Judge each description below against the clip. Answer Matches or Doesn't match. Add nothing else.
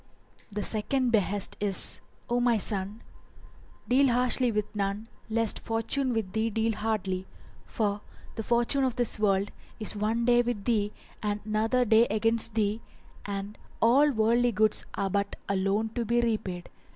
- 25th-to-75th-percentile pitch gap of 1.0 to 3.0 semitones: Matches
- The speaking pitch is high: Matches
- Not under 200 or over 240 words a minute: Doesn't match